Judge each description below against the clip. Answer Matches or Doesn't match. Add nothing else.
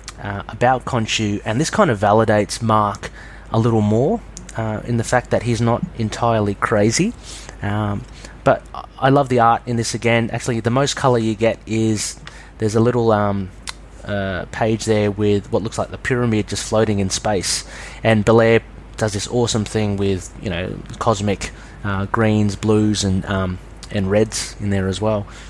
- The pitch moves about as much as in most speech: Doesn't match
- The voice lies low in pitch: Matches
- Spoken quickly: Doesn't match